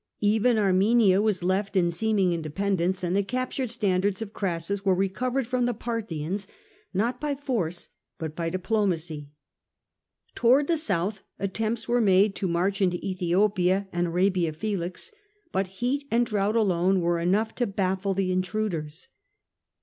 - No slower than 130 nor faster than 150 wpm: Yes, average, 145 wpm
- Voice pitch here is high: Yes, high, 195 Hz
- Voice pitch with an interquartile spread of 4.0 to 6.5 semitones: No, average, 3.5 semitones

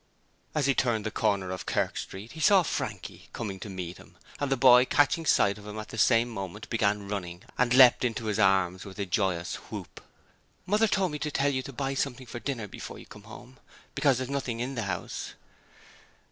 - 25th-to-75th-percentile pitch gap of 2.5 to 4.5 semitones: No, average, 5.2 semitones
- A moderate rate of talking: No, fast, 215 wpm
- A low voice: Yes, low, 115 Hz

